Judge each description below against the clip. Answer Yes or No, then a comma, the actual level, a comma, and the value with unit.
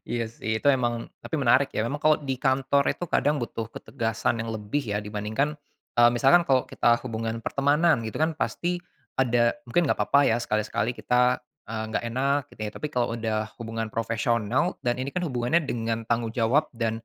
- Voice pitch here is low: Yes, low, 120 Hz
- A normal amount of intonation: Yes, average, 3.5 semitones